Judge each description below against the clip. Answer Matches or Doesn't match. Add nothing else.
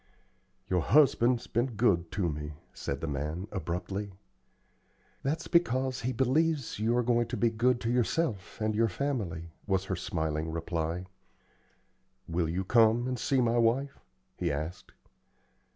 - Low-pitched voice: Matches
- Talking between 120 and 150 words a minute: Matches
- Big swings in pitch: Matches